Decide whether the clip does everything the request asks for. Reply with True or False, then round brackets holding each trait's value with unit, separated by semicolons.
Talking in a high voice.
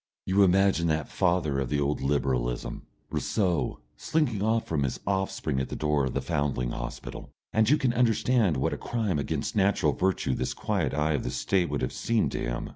False (80 Hz)